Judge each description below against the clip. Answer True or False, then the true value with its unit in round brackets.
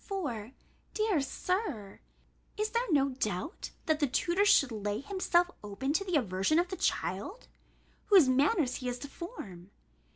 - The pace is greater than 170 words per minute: False (155 wpm)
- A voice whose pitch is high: True (290 Hz)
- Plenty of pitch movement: True (8.5 semitones)